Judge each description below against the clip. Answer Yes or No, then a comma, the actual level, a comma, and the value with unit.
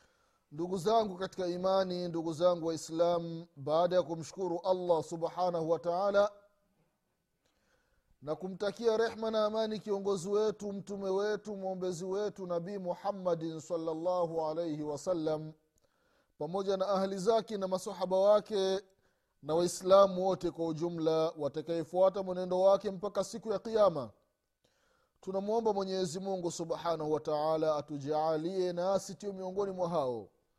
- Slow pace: No, average, 115 wpm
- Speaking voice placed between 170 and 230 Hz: Yes, medium, 185 Hz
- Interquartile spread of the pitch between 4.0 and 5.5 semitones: No, average, 3.1 semitones